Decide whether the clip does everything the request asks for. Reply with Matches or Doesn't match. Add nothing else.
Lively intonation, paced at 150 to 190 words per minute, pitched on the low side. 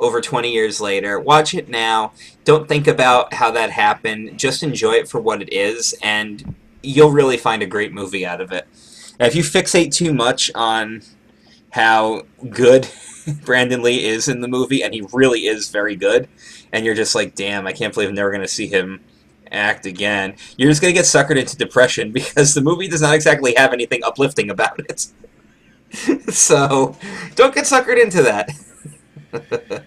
Matches